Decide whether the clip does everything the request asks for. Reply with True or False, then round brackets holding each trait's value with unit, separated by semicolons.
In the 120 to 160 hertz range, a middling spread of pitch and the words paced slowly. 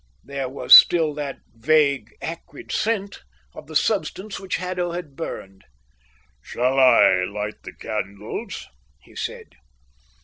False (140 Hz; 7.4 semitones; 125 wpm)